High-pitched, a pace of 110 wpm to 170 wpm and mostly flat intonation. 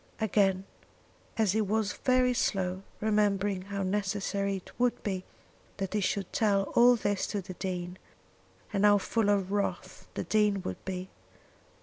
Yes: high, 200 Hz; average, 145 wpm; narrow, 1.9 semitones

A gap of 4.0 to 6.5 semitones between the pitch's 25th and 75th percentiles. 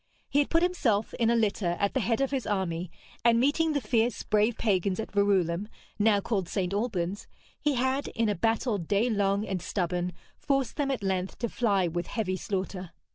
Yes: average, 4.3 semitones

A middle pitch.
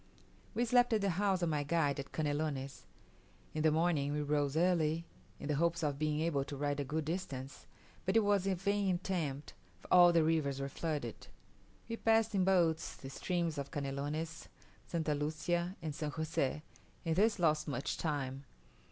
Yes: medium, 160 Hz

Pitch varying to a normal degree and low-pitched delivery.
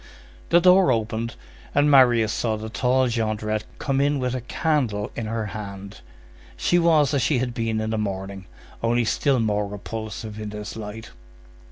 Yes: average, 3.3 semitones; low, 115 Hz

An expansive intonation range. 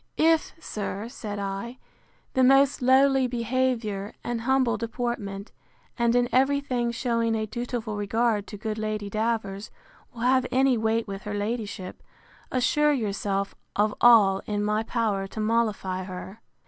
No: average, 3.0 semitones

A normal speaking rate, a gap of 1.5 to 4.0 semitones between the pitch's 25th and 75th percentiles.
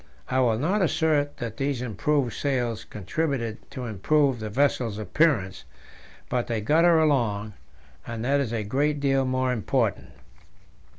No: average, 145 wpm; average, 4.4 semitones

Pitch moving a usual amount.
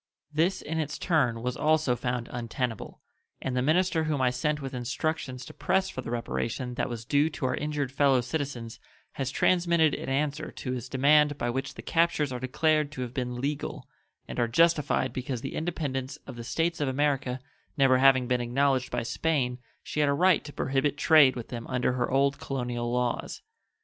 Yes: average, 3.3 semitones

